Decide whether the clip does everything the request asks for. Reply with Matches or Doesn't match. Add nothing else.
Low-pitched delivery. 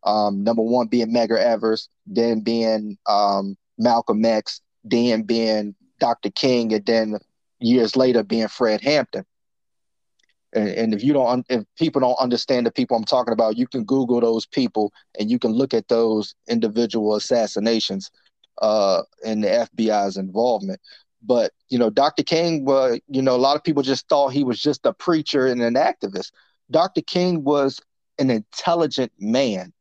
Matches